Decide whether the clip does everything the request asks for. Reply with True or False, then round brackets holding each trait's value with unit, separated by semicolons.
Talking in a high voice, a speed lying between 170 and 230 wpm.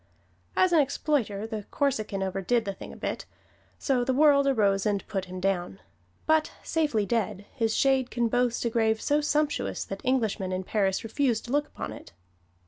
True (230 Hz; 180 wpm)